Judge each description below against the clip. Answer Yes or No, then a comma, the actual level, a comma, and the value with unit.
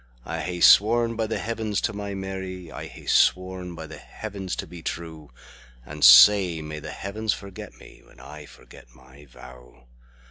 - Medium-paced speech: Yes, average, 155 wpm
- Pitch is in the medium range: No, very low, 90 Hz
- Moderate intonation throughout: Yes, average, 5.0 semitones